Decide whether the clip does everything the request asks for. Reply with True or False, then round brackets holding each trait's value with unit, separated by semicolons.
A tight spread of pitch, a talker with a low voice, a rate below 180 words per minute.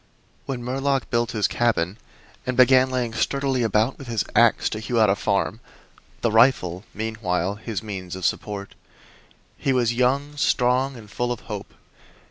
False (3.3 semitones; 120 Hz; 160 wpm)